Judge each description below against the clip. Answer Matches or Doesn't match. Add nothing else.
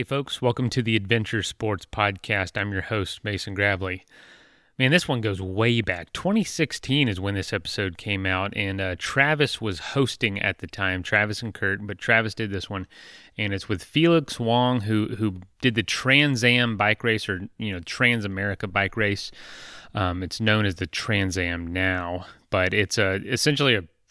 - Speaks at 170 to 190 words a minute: Matches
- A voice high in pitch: Doesn't match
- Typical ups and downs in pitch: Matches